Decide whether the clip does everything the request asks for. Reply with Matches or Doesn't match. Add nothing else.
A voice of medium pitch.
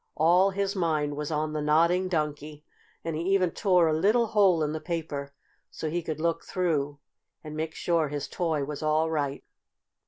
Matches